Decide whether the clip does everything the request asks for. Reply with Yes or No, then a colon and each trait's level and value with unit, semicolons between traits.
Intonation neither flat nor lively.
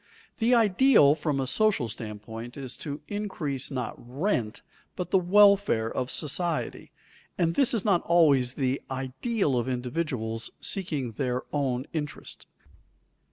No: wide, 6.5 semitones